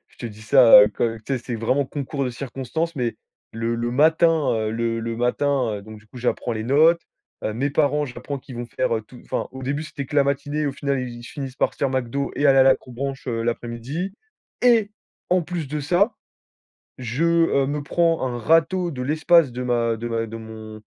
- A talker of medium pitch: No, low, 130 Hz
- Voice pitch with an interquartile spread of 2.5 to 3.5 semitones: No, average, 4.0 semitones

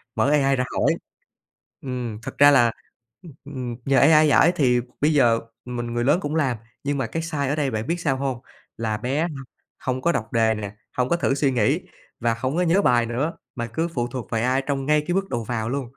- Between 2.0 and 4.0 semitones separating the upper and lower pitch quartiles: Yes, average, 3.7 semitones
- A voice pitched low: Yes, low, 130 Hz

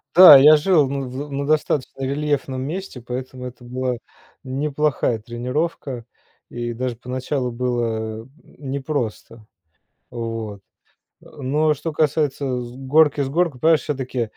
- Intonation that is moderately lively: Yes, average, 3.2 semitones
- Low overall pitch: Yes, low, 130 Hz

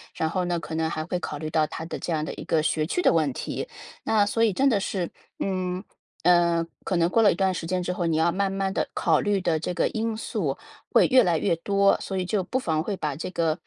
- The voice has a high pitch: No, medium, 180 Hz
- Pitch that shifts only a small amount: No, average, 3.3 semitones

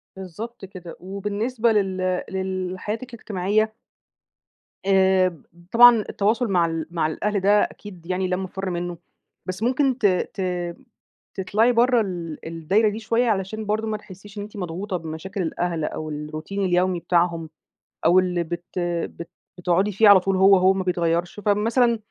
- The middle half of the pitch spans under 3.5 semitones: Yes, average, 3.1 semitones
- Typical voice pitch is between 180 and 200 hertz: Yes, high, 190 Hz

